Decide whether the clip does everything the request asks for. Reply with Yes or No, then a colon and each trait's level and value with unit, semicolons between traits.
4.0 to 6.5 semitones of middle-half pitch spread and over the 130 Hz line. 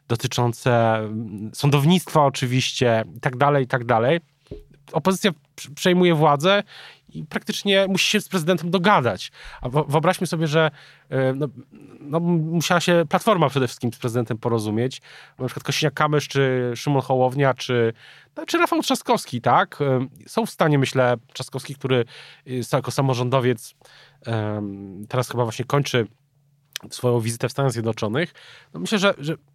Yes: average, 4.8 semitones; medium, 140 Hz